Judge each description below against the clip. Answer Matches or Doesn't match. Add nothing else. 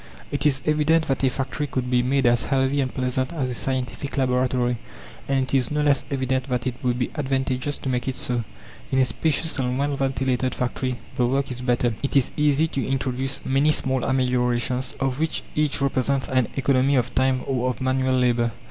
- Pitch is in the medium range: Doesn't match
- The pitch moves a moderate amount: Doesn't match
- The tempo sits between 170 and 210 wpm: Matches